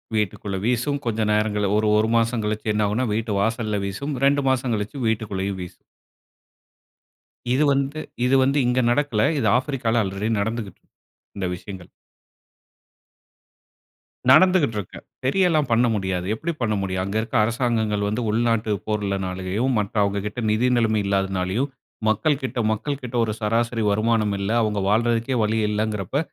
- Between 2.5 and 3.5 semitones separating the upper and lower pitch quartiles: Yes, average, 3.2 semitones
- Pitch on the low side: Yes, low, 110 Hz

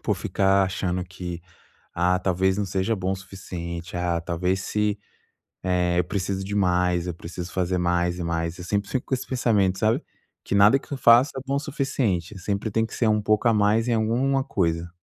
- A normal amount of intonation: Yes, average, 3.4 semitones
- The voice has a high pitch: No, very low, 95 Hz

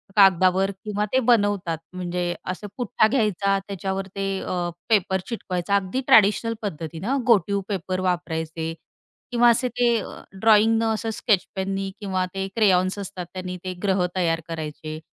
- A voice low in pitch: No, high, 195 Hz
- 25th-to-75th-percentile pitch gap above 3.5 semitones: No, average, 2.9 semitones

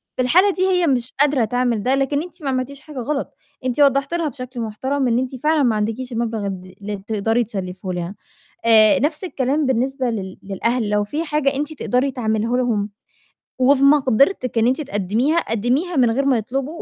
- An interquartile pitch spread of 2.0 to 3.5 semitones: No, average, 4.0 semitones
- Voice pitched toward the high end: Yes, very high, 255 Hz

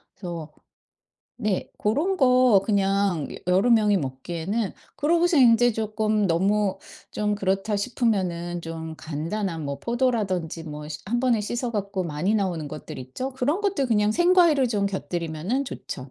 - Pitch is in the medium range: No, high, 205 Hz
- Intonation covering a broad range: Yes, wide, 5.8 semitones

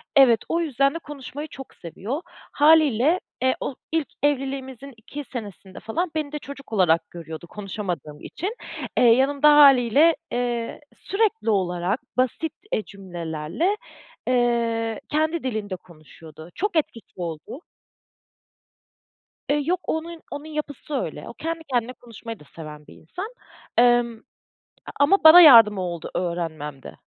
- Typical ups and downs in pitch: No, wide, 7.7 semitones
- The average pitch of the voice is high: Yes, high, 245 Hz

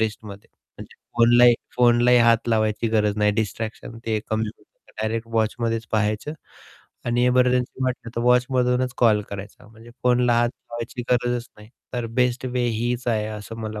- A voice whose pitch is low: Yes, low, 115 Hz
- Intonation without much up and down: Yes, narrow, 2.0 semitones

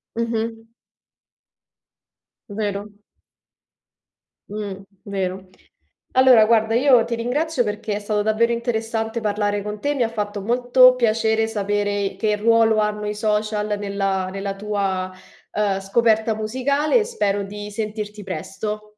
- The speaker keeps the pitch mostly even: Yes, narrow, 2.0 semitones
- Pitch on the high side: Yes, high, 215 Hz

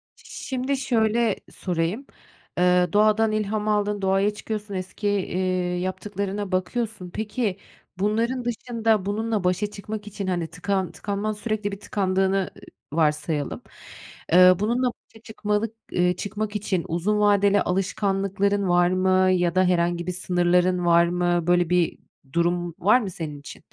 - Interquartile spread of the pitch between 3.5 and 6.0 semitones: No, average, 2.9 semitones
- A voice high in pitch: Yes, high, 195 Hz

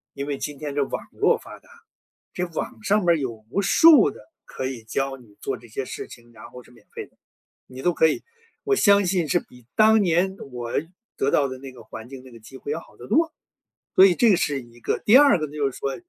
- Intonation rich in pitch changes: Yes, wide, 6.6 semitones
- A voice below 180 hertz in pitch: Yes, medium, 140 Hz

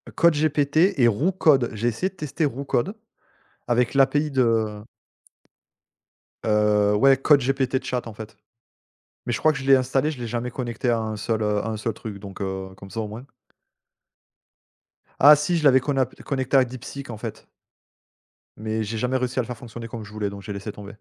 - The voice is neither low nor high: No, low, 120 Hz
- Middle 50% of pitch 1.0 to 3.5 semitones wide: No, average, 4.1 semitones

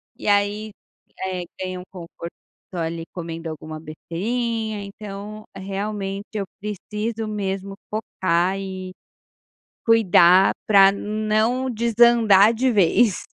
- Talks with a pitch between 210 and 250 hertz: No, high, 200 Hz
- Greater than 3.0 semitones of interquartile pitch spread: No, average, 2.7 semitones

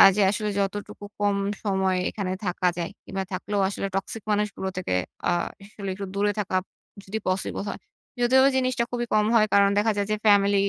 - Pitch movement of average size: No, narrow, 1.5 semitones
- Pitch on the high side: Yes, high, 200 Hz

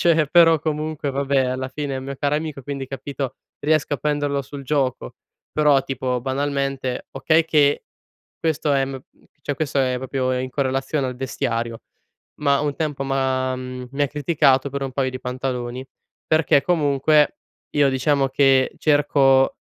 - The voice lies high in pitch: No, medium, 140 Hz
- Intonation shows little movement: Yes, narrow, 2.0 semitones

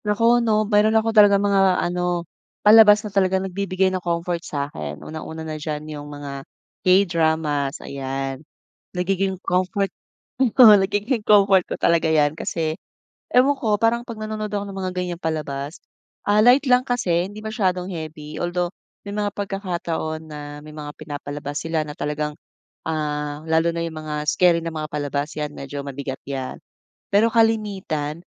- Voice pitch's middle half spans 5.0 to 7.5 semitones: Yes, average, 5.3 semitones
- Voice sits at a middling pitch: Yes, medium, 175 Hz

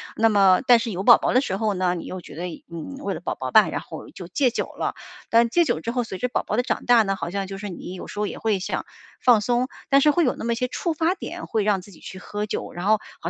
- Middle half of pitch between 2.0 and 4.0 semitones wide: No, average, 4.7 semitones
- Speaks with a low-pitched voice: No, high, 215 Hz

